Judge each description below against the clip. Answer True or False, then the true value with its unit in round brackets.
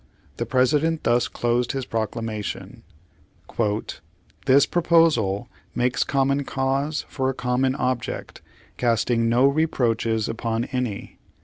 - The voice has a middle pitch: False (125 Hz)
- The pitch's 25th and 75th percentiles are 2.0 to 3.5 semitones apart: True (3.1 semitones)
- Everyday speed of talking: False (110 wpm)